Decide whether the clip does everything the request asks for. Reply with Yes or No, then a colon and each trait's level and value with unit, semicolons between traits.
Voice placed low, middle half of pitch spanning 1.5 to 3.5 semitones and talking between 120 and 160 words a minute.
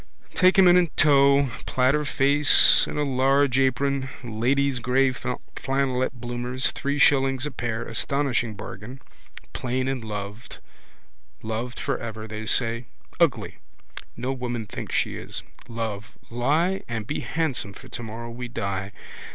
Yes: low, 125 Hz; average, 3.1 semitones; slow, 135 wpm